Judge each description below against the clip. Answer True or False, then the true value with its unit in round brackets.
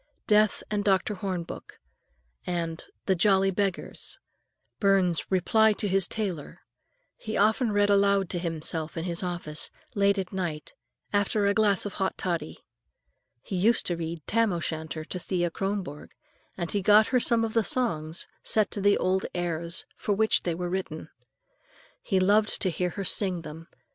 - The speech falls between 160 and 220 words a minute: True (165 wpm)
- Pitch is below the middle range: False (190 Hz)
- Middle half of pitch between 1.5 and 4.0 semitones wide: True (3.1 semitones)